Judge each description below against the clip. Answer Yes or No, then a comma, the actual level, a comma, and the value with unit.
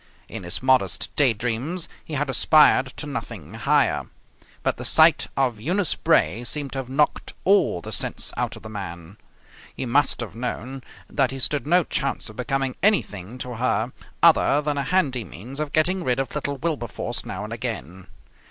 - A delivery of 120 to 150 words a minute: No, average, 180 wpm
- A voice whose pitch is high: No, low, 130 Hz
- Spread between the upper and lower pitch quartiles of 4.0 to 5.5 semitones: Yes, average, 4.7 semitones